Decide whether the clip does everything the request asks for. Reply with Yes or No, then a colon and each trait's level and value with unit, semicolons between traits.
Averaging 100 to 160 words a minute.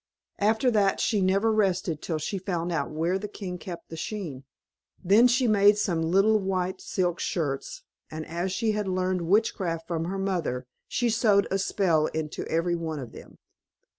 No: average, 180 wpm